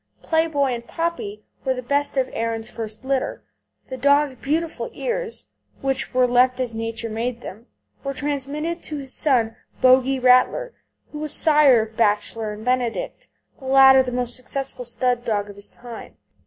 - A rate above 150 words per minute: Yes, average, 170 wpm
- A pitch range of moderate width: Yes, average, 3.4 semitones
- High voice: Yes, very high, 255 Hz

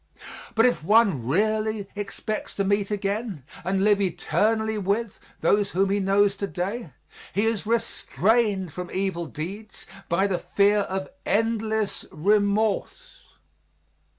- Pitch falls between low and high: No, high, 205 Hz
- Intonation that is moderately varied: No, narrow, 2.1 semitones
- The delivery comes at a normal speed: No, slow, 125 wpm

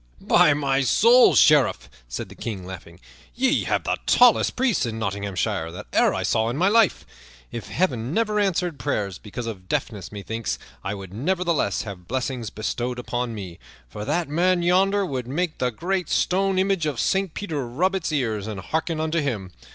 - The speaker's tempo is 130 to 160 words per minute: No, average, 180 wpm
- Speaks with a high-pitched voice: No, low, 135 Hz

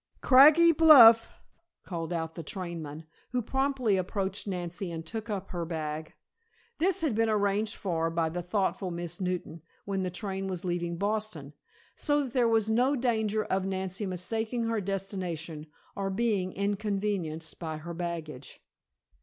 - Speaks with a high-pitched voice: Yes, high, 195 Hz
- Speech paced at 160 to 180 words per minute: No, average, 150 wpm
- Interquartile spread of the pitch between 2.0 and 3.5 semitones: No, average, 4.4 semitones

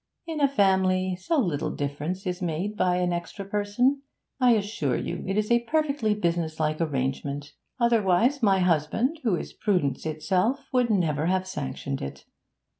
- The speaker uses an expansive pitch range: Yes, wide, 6.1 semitones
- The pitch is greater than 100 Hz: Yes, medium, 185 Hz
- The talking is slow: No, average, 155 wpm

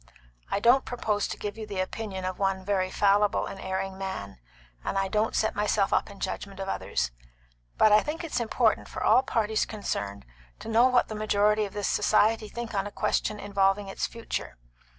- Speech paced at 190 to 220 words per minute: Yes, average, 195 wpm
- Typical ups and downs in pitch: No, narrow, 2.1 semitones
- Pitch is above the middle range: Yes, high, 205 Hz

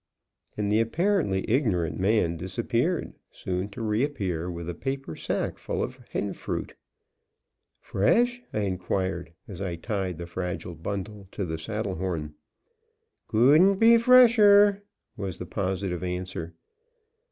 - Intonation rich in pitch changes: Yes, wide, 6.3 semitones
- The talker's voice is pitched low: Yes, low, 100 Hz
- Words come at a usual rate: No, slow, 130 wpm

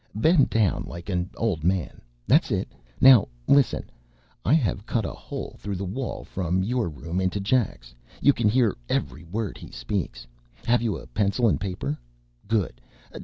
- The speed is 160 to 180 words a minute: Yes, average, 165 wpm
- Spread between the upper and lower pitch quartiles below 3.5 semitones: No, average, 4.9 semitones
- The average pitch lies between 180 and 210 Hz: No, low, 100 Hz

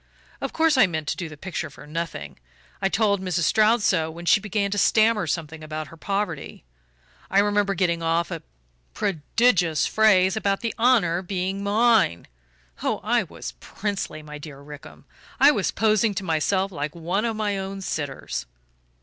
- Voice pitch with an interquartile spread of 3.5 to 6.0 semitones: Yes, average, 4.4 semitones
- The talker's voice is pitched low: No, high, 190 Hz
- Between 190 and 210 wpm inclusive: No, average, 170 wpm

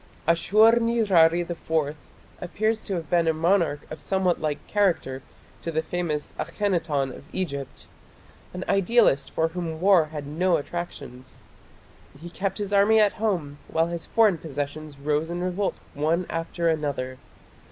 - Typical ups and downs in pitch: Yes, average, 3.9 semitones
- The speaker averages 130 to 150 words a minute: Yes, average, 145 wpm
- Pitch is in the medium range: Yes, medium, 170 Hz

